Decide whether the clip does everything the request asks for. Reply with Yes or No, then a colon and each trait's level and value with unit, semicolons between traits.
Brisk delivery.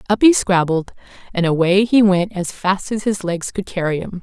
Yes: fast, 215 wpm